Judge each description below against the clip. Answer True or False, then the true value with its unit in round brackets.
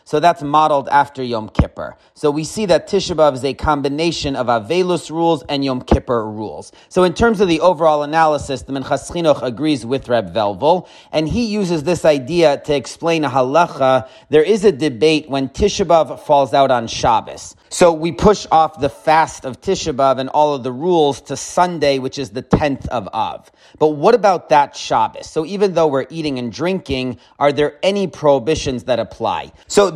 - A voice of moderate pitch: True (150 Hz)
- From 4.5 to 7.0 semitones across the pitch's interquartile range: False (3.7 semitones)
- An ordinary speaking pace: True (190 wpm)